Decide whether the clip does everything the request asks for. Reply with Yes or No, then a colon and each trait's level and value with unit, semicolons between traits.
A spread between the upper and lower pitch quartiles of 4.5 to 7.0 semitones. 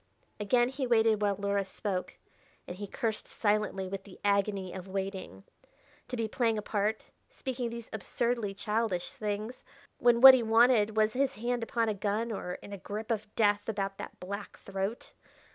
No: average, 2.7 semitones